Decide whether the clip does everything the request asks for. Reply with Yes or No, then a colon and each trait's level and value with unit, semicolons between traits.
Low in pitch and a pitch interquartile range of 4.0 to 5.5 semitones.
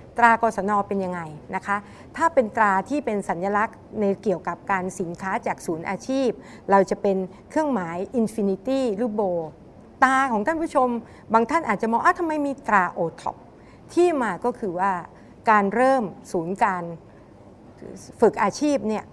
No: high, 210 Hz; average, 4.4 semitones